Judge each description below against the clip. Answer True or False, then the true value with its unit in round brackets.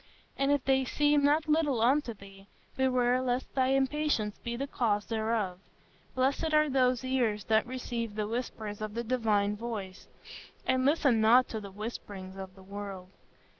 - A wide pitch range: False (4.1 semitones)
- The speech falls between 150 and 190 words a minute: True (165 wpm)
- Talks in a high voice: True (235 Hz)